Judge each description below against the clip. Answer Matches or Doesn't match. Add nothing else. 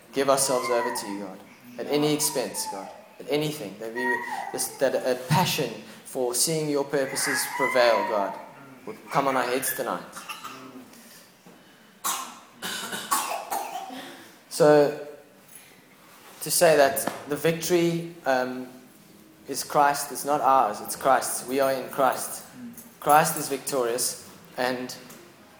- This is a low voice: Doesn't match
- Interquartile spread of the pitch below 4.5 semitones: Matches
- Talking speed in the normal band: Doesn't match